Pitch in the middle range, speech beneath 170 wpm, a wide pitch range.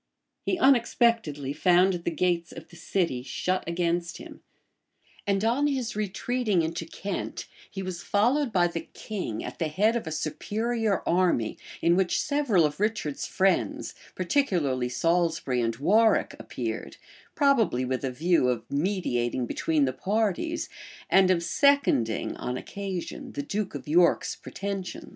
Yes: medium, 180 Hz; average, 145 wpm; wide, 5.8 semitones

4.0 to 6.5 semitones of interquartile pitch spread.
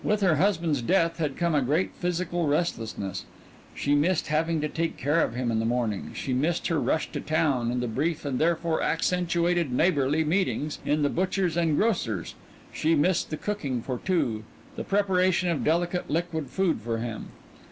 Yes: average, 4.6 semitones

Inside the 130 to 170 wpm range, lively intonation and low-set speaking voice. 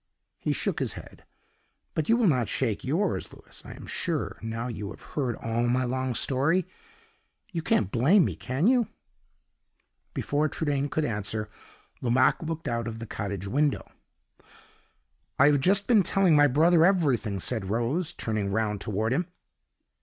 Yes: average, 160 wpm; wide, 6.1 semitones; low, 130 Hz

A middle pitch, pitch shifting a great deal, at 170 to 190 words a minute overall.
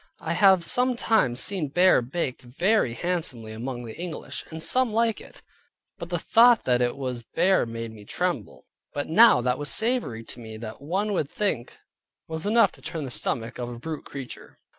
Yes: medium, 150 Hz; wide, 8.0 semitones; average, 185 wpm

